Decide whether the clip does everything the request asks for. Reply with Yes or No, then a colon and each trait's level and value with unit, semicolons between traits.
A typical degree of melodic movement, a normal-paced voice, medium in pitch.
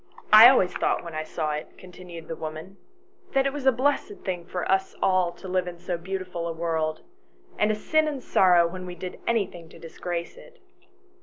No: average, 4.2 semitones; fast, 215 wpm; medium, 180 Hz